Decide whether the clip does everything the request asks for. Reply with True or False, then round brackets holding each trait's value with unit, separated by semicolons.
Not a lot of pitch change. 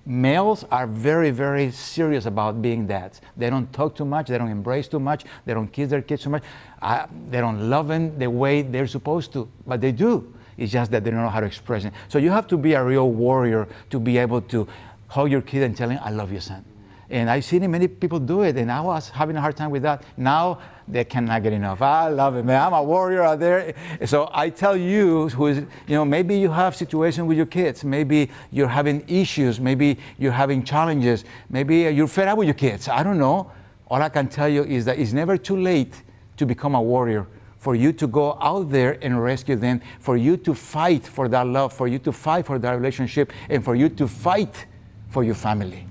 False (4.0 semitones)